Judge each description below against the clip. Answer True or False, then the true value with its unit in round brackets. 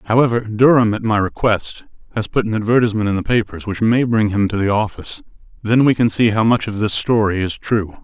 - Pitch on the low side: True (110 Hz)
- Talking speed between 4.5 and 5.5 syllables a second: False (5.8 syllables/s)